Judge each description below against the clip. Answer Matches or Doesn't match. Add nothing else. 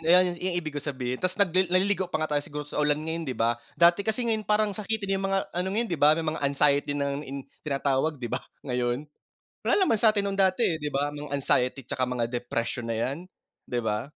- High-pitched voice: Doesn't match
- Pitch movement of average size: Doesn't match